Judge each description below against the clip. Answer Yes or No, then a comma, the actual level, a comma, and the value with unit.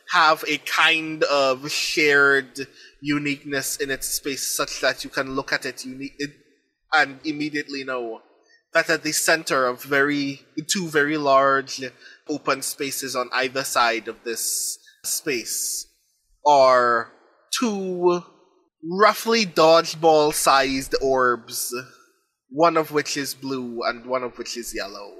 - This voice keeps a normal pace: No, slow, 130 wpm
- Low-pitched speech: No, medium, 145 Hz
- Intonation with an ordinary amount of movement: Yes, average, 3.5 semitones